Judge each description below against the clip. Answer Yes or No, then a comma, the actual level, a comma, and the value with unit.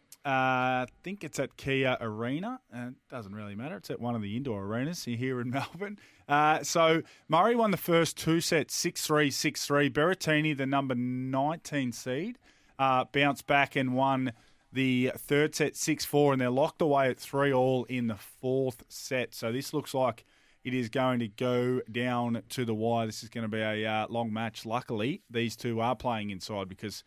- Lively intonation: No, average, 3.6 semitones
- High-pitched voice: No, low, 130 Hz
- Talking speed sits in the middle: Yes, average, 190 wpm